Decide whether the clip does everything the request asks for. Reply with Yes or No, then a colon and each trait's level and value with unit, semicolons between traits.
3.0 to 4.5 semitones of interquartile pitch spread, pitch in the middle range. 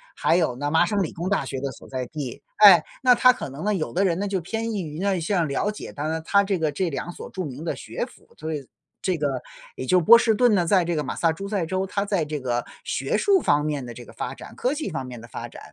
No: wide, 5.5 semitones; medium, 170 Hz